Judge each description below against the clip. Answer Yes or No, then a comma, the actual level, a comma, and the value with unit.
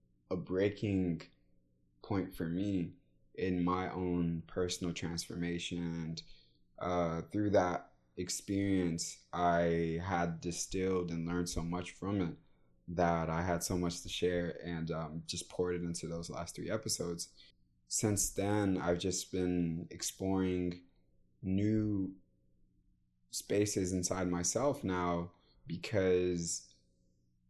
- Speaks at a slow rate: Yes, slow, 115 wpm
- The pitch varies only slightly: Yes, narrow, 2.1 semitones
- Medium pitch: No, very low, 85 Hz